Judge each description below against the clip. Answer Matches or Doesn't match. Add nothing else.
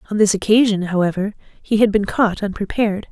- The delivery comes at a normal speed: Matches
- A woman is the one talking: Matches